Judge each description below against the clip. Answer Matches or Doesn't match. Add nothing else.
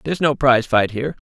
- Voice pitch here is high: Doesn't match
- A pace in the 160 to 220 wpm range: Doesn't match